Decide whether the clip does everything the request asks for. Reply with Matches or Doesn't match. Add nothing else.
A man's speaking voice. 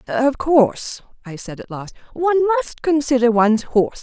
Doesn't match